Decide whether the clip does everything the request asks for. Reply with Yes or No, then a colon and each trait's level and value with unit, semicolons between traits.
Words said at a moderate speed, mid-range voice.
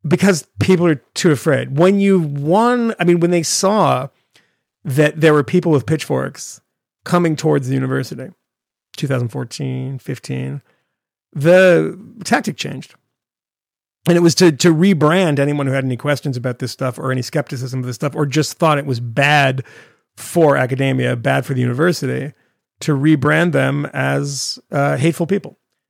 Yes: average, 155 wpm; medium, 145 Hz